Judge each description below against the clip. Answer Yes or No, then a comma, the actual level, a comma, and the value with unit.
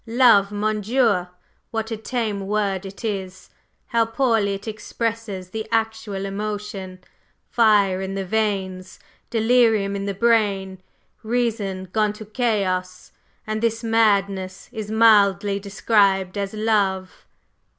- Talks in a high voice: Yes, high, 210 Hz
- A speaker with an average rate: No, slow, 120 wpm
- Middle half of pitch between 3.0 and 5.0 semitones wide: No, narrow, 2.4 semitones